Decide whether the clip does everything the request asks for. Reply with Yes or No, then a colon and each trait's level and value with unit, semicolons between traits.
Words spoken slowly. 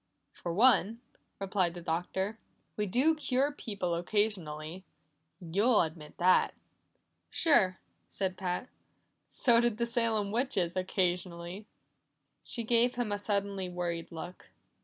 Yes: slow, 115 wpm